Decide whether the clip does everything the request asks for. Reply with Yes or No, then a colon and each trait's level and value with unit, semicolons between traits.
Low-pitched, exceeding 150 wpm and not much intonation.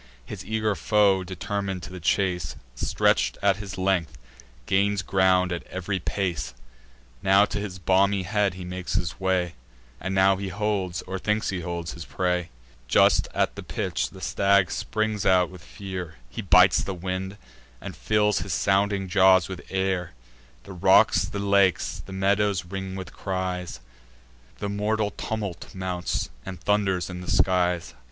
Yes: very low, 95 Hz; average, 160 wpm; narrow, 1.7 semitones